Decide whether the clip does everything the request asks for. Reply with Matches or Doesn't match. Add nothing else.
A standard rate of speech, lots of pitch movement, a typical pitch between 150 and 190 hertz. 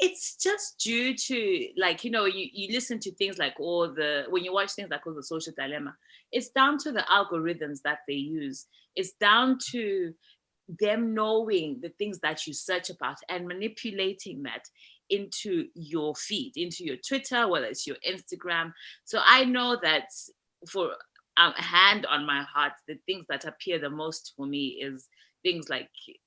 Matches